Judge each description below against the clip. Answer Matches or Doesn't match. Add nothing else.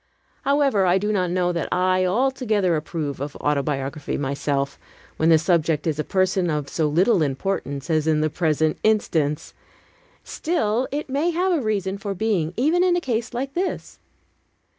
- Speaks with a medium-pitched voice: Matches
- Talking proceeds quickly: Doesn't match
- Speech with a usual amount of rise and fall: Doesn't match